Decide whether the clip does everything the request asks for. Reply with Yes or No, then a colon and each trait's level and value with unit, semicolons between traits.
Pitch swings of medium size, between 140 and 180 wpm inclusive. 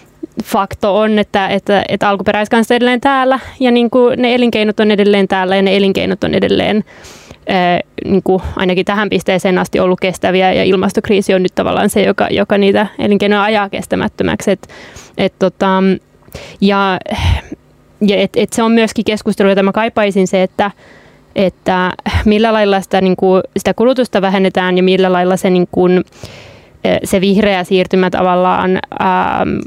No: narrow, 2.2 semitones; fast, 155 wpm